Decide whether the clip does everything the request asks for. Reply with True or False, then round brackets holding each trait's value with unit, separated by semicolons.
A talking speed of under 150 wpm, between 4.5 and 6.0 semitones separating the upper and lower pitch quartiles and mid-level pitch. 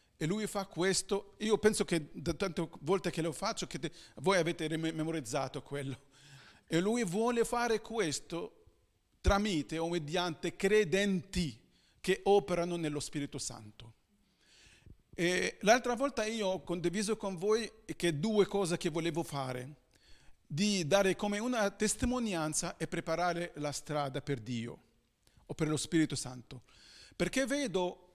True (140 wpm; 5.3 semitones; 175 Hz)